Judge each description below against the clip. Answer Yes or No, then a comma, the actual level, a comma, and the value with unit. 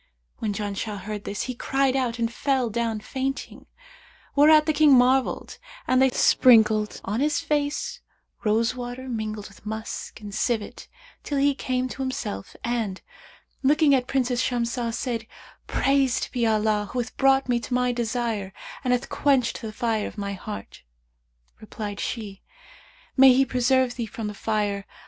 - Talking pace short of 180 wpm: Yes, average, 160 wpm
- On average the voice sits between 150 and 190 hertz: No, high, 240 Hz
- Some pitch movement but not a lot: Yes, average, 3.5 semitones